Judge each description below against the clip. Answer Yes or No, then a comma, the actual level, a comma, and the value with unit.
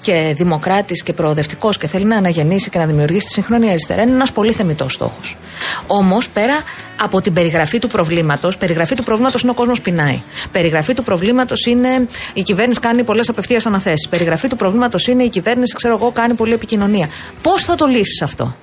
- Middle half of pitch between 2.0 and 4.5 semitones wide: No, wide, 5.5 semitones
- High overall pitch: Yes, high, 205 Hz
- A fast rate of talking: Yes, fast, 190 wpm